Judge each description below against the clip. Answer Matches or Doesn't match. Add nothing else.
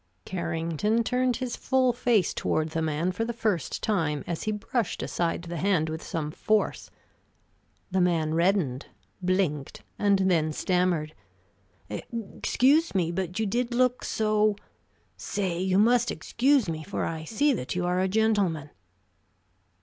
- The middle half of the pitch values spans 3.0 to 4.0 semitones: Doesn't match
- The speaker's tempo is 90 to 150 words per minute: Matches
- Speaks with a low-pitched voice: Doesn't match